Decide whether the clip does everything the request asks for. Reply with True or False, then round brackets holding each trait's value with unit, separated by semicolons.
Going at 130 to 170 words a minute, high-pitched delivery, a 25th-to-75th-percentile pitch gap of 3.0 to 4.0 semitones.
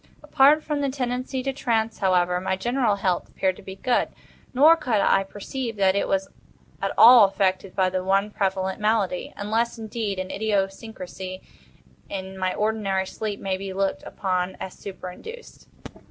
True (155 wpm; 200 Hz; 3.5 semitones)